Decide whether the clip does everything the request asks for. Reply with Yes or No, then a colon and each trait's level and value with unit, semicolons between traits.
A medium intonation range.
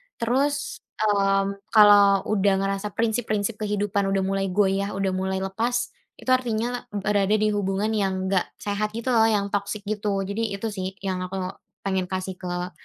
No: narrow, 1.8 semitones